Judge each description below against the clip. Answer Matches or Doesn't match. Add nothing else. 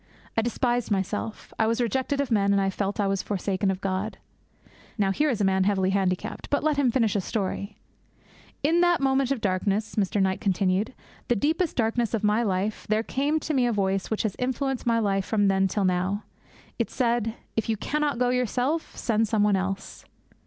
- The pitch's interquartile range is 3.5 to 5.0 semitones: Matches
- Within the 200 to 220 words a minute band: Matches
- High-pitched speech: Matches